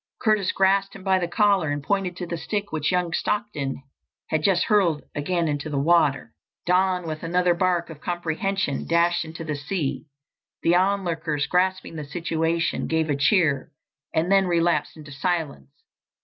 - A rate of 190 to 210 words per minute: No, average, 165 wpm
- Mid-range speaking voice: Yes, medium, 170 Hz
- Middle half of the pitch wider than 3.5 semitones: No, average, 3.2 semitones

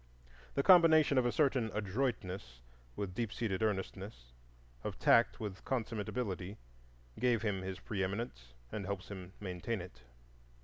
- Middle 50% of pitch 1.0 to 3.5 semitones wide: No, average, 4.1 semitones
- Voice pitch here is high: No, low, 105 Hz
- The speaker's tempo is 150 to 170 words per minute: No, slow, 135 wpm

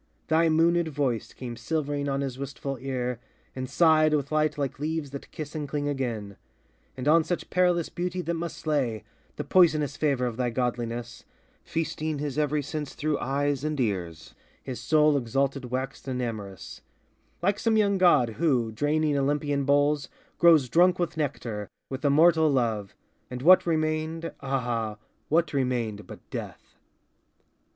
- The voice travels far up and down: No, average, 3.8 semitones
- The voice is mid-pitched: Yes, medium, 145 Hz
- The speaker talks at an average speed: Yes, average, 155 wpm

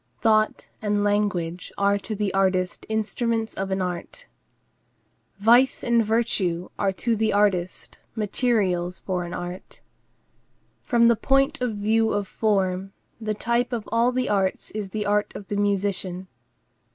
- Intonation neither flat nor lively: Yes, average, 3.0 semitones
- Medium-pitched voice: No, high, 205 Hz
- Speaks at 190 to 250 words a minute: No, average, 145 wpm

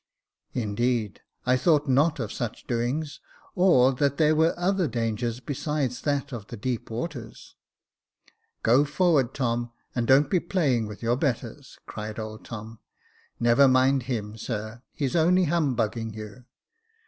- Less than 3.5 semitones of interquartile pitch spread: No, average, 4.2 semitones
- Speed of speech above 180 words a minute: No, average, 150 wpm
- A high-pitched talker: No, low, 125 Hz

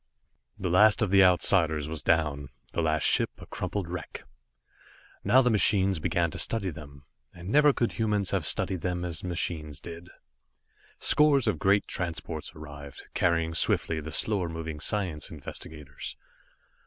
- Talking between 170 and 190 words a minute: No, average, 155 wpm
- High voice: No, very low, 85 Hz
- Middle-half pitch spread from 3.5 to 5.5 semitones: Yes, average, 3.9 semitones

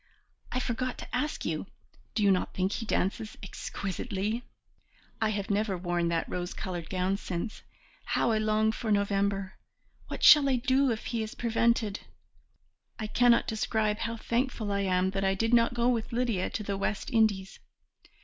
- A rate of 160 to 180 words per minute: Yes, average, 170 wpm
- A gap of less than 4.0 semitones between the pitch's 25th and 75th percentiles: Yes, average, 3.2 semitones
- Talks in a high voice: Yes, high, 215 Hz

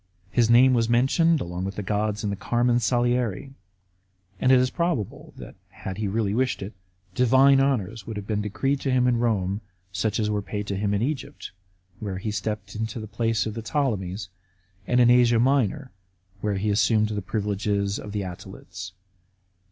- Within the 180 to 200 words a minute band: Yes, average, 190 wpm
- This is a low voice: Yes, low, 110 Hz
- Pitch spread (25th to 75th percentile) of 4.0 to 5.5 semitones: No, average, 3.5 semitones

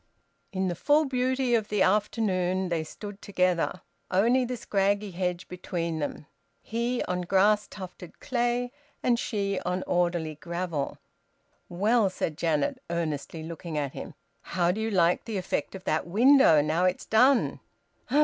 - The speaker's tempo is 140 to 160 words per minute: Yes, average, 150 wpm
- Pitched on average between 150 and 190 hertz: Yes, medium, 185 Hz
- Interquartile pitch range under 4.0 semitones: No, average, 4.4 semitones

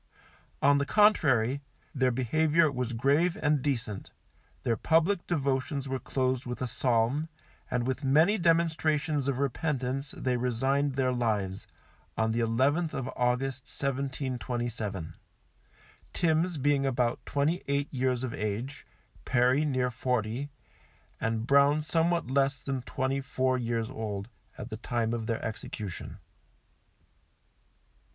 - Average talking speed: No, slow, 125 wpm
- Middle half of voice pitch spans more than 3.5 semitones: No, average, 3.2 semitones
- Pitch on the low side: Yes, low, 130 Hz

